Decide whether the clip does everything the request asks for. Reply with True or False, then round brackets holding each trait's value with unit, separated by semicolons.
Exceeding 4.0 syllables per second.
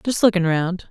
True (5.1 syllables/s)